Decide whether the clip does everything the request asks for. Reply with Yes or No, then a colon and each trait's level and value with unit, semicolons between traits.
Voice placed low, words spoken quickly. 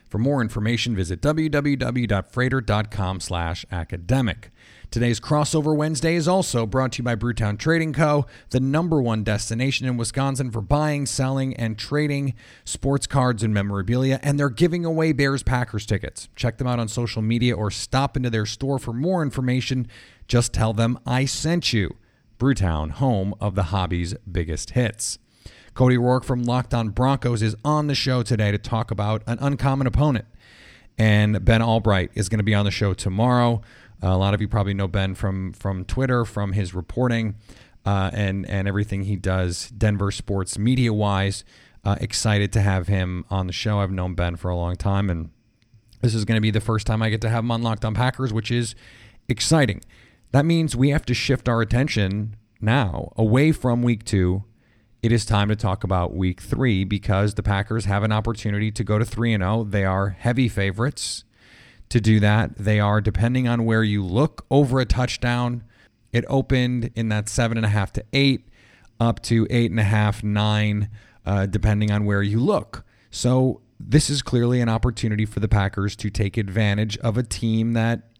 No: low, 115 Hz; average, 180 wpm